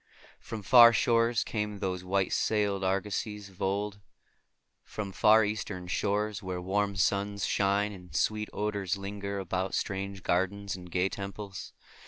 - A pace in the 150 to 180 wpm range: No, average, 140 wpm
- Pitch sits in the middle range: No, low, 100 Hz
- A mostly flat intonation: Yes, narrow, 1.5 semitones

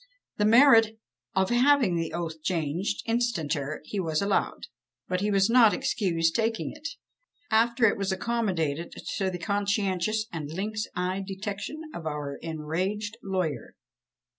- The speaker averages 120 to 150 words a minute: Yes, average, 140 wpm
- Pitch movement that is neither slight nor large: Yes, average, 4.8 semitones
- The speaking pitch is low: No, high, 195 Hz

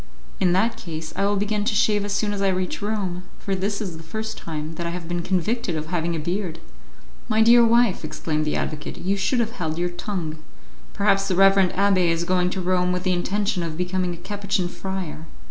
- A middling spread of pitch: Yes, average, 3.0 semitones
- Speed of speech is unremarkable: No, fast, 220 wpm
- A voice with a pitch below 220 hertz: Yes, medium, 185 Hz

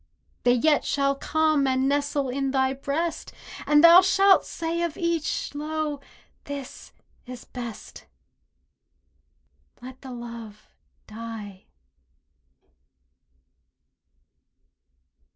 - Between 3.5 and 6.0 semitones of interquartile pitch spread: Yes, average, 3.9 semitones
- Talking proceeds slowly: Yes, slow, 90 wpm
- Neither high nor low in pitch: No, very high, 280 Hz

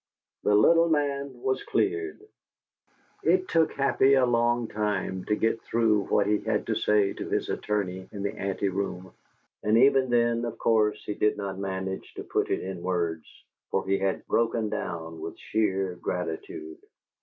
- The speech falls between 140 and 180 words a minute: Yes, average, 165 wpm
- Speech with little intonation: No, average, 4.1 semitones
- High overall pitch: No, low, 105 Hz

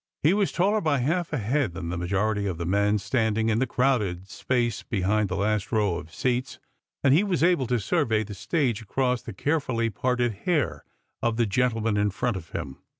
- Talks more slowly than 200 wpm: No, fast, 205 wpm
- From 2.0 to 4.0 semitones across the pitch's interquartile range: No, average, 4.6 semitones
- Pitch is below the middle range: Yes, low, 115 Hz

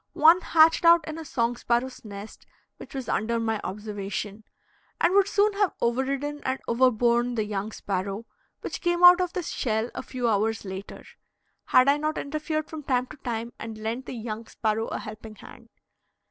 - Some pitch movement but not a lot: No, wide, 5.9 semitones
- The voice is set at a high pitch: Yes, high, 240 Hz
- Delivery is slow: No, average, 180 wpm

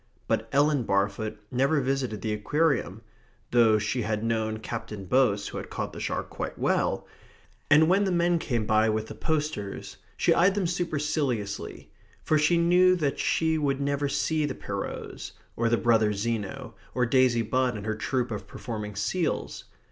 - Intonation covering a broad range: Yes, wide, 5.7 semitones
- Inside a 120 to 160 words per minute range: No, average, 170 wpm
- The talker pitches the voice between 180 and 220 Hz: No, low, 125 Hz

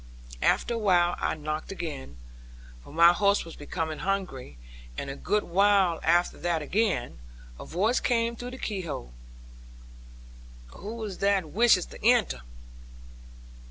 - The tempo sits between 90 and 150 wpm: Yes, average, 140 wpm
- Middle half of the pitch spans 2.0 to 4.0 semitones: No, average, 4.7 semitones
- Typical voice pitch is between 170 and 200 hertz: Yes, medium, 185 Hz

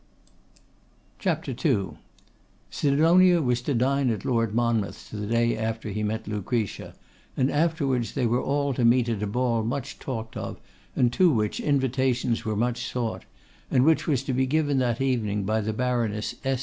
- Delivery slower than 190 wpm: Yes, average, 160 wpm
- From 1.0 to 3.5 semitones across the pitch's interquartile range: Yes, average, 3.2 semitones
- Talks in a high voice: No, low, 120 Hz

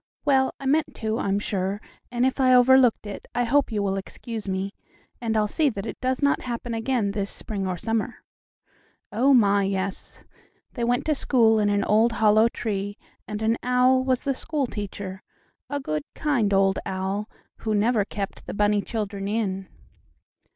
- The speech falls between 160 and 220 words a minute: Yes, average, 180 wpm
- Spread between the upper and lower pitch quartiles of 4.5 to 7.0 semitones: No, average, 3.8 semitones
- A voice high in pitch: Yes, high, 220 Hz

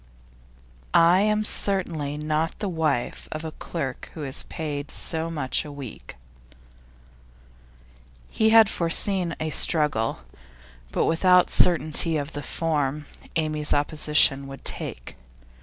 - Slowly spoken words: Yes, slow, 120 wpm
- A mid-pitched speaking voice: Yes, medium, 155 Hz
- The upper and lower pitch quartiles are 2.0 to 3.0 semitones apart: Yes, average, 2.7 semitones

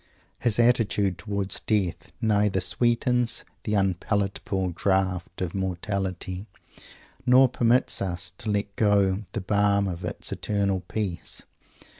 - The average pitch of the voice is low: Yes, low, 100 Hz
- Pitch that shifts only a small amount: Yes, narrow, 2.3 semitones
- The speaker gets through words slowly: Yes, slow, 115 wpm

